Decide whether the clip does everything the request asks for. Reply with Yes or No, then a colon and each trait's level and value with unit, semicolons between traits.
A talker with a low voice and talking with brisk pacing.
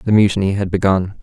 No: low, 100 Hz; average, 195 wpm